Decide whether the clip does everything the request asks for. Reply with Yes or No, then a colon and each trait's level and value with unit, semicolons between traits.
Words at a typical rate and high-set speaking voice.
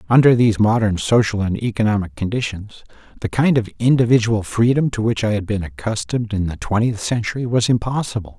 No: average, 170 wpm; low, 110 Hz